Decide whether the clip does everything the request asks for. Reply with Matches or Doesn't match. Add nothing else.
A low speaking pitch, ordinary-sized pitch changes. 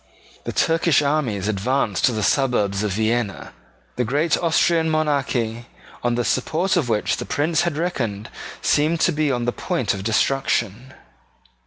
Doesn't match